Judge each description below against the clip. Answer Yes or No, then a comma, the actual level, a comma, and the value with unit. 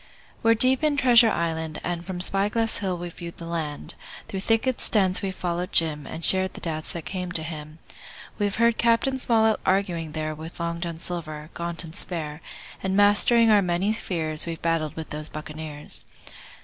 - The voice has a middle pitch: Yes, medium, 175 Hz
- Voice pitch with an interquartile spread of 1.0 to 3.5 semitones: No, average, 4.2 semitones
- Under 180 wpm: No, average, 185 wpm